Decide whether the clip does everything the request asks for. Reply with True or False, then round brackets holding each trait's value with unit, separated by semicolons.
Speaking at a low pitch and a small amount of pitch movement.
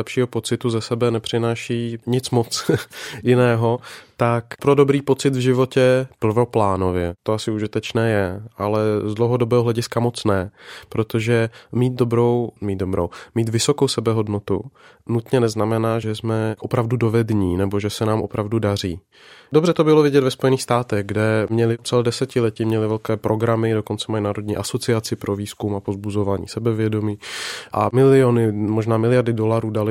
True (115 Hz; 2.2 semitones)